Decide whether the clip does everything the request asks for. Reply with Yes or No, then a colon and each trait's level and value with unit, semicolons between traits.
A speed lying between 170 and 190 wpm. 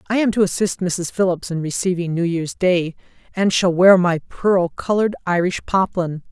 Yes: average, 180 wpm